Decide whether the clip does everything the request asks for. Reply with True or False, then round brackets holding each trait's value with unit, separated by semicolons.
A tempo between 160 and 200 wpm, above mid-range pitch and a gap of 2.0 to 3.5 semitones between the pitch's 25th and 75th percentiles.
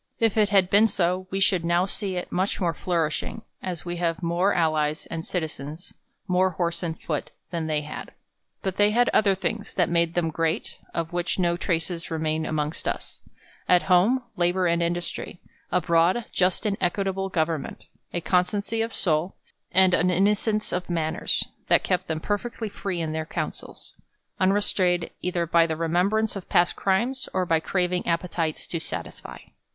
False (175 wpm; 175 Hz; 2.6 semitones)